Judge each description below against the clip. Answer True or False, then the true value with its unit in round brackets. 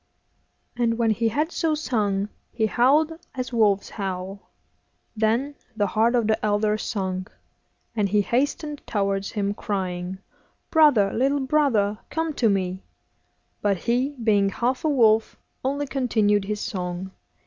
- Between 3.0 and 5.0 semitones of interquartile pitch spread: True (4.6 semitones)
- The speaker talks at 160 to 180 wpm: False (135 wpm)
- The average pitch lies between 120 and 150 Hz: False (220 Hz)